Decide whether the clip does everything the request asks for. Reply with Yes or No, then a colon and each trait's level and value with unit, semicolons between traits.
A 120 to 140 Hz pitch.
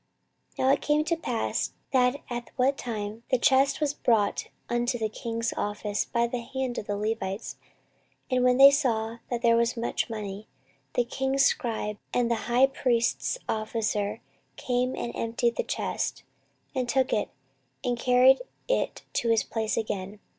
No: high, 235 Hz